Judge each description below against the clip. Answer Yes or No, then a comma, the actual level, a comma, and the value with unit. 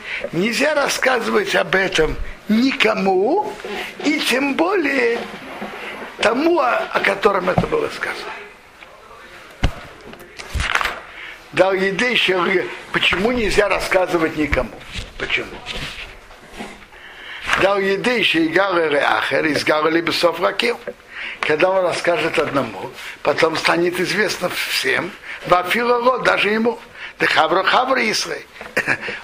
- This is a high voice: Yes, high, 205 Hz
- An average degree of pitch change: No, wide, 6.6 semitones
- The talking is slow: Yes, slow, 75 wpm